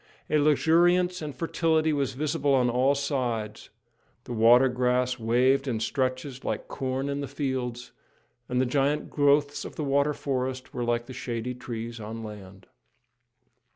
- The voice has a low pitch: Yes, low, 130 Hz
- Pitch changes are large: No, average, 2.8 semitones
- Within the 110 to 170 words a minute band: Yes, average, 155 wpm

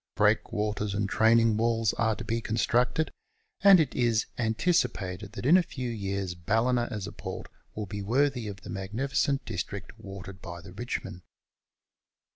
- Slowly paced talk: No, average, 155 wpm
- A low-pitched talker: Yes, low, 110 Hz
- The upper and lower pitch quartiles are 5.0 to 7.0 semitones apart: No, average, 3.5 semitones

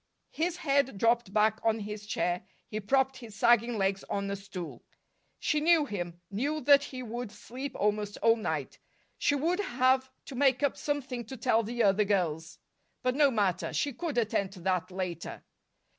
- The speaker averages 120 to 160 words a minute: No, average, 175 wpm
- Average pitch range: Yes, average, 5.0 semitones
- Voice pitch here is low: No, high, 230 Hz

